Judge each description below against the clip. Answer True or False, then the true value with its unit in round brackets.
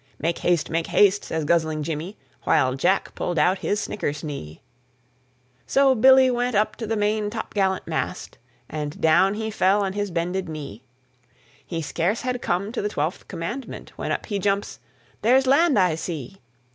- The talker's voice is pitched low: False (190 Hz)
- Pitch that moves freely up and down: False (5.0 semitones)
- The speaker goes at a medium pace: True (165 wpm)